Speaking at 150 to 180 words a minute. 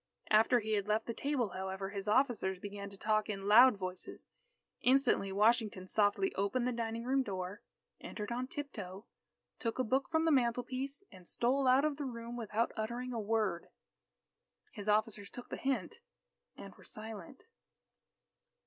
Yes: average, 165 wpm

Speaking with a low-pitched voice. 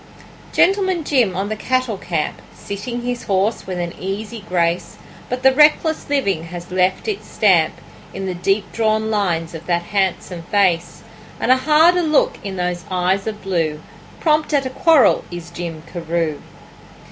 No: high, 195 Hz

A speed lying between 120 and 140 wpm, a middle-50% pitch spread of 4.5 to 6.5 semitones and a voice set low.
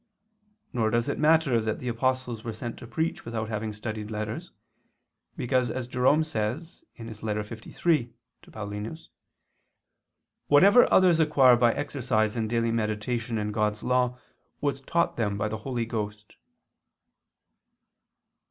No: slow, 135 wpm; average, 3.2 semitones; low, 115 Hz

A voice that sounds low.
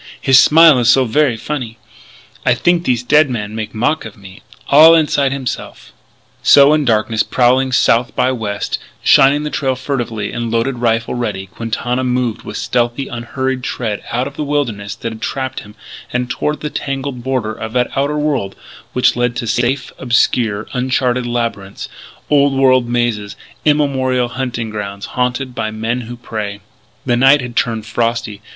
Yes: low, 125 Hz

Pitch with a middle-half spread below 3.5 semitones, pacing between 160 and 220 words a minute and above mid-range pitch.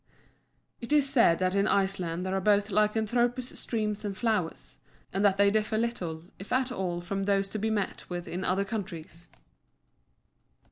Yes: average, 2.9 semitones; average, 170 wpm; high, 200 Hz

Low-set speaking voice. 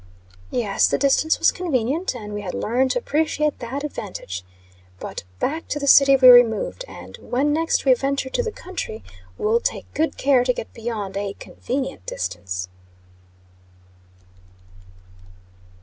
No: very high, 255 Hz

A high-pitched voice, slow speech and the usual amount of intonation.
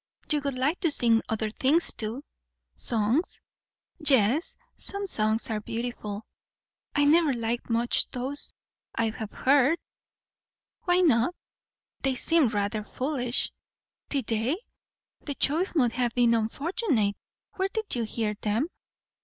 Yes: very high, 250 Hz; slow, 130 wpm; average, 4.9 semitones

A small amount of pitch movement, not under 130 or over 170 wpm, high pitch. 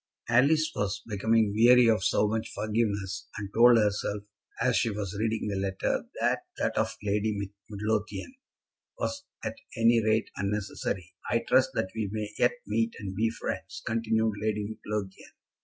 No: narrow, 1.9 semitones; average, 155 wpm; low, 110 Hz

